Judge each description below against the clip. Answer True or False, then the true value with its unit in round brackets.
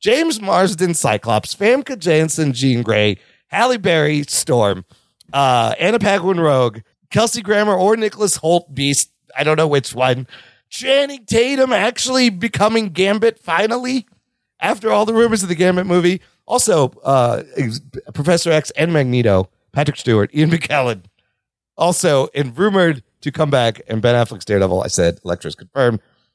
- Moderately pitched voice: True (160 Hz)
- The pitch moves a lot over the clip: True (8.7 semitones)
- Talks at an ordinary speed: True (145 wpm)